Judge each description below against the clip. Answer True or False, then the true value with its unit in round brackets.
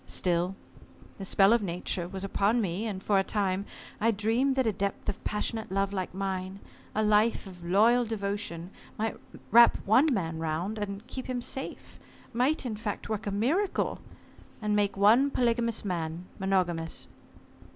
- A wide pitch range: False (3.2 semitones)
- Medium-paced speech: True (160 wpm)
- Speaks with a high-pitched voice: True (205 Hz)